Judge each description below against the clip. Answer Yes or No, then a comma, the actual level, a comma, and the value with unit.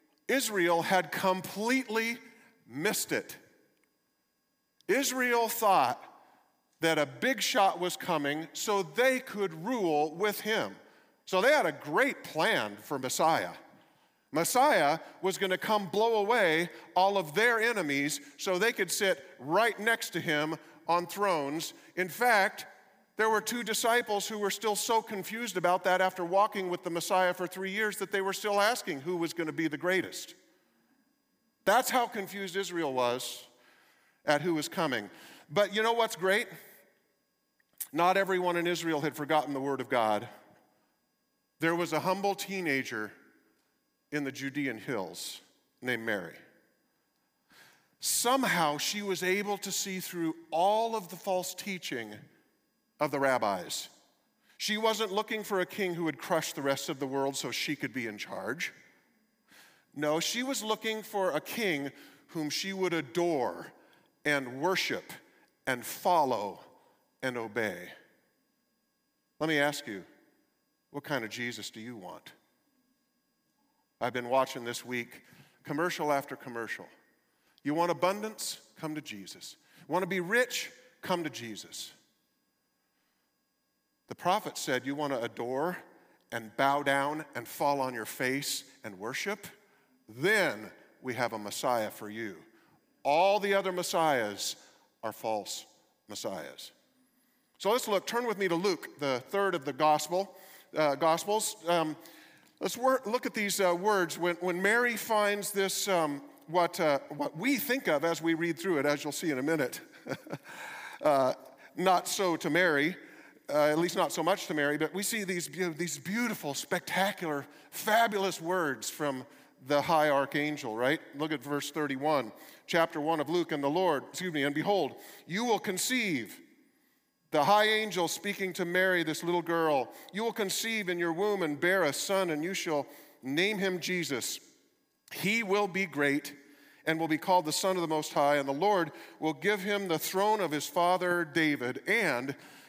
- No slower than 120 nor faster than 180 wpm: Yes, average, 160 wpm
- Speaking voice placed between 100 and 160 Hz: No, medium, 180 Hz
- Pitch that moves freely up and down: Yes, wide, 5.7 semitones